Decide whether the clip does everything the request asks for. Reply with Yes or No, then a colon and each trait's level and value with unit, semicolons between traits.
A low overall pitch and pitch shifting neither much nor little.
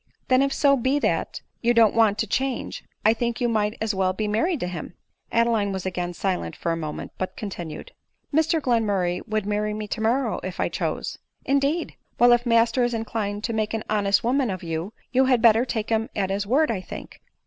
No: high, 220 Hz; average, 3.4 semitones